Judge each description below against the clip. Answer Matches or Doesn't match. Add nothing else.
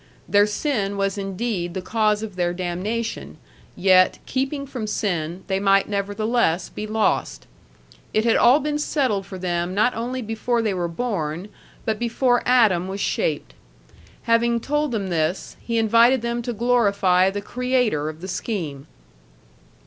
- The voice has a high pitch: Matches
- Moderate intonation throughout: Matches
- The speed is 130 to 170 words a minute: Matches